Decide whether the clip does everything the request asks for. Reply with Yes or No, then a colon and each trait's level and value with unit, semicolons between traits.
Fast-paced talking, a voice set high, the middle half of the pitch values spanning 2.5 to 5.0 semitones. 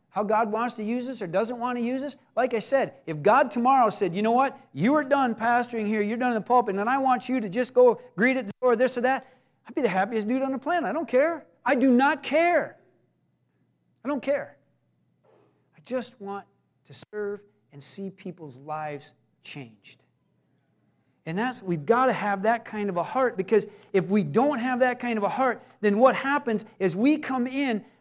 Yes: fast, 220 wpm; high, 240 Hz; average, 4.4 semitones